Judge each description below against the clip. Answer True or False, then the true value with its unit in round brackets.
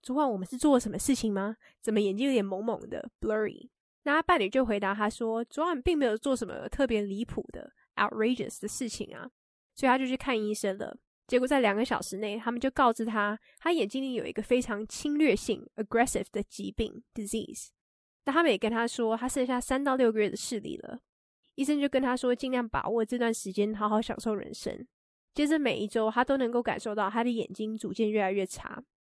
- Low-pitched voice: False (230 Hz)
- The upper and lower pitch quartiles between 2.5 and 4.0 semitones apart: True (3.6 semitones)